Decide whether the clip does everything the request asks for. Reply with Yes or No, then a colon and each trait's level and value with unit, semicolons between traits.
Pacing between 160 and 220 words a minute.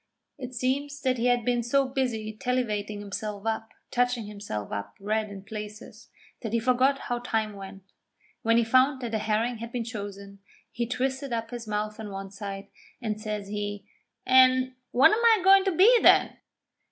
Yes: average, 180 wpm